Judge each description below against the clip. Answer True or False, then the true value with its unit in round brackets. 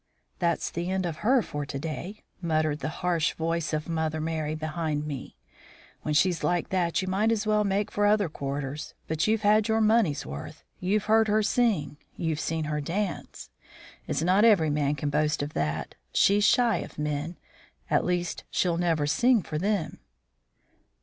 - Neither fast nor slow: True (175 wpm)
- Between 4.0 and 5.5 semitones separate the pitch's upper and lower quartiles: True (5.2 semitones)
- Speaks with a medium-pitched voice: True (170 Hz)